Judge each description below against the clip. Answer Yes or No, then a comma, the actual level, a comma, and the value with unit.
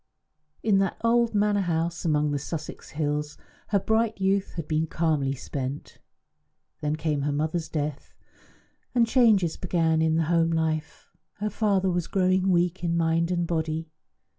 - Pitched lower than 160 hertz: No, medium, 165 Hz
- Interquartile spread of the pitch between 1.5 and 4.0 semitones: Yes, average, 3.6 semitones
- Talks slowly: No, average, 155 wpm